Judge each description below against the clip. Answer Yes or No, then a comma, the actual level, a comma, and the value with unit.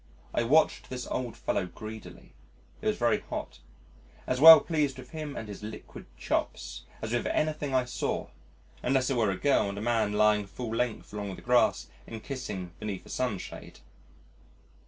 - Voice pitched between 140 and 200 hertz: No, low, 120 Hz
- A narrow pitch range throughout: No, average, 3.7 semitones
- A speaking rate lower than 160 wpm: No, average, 175 wpm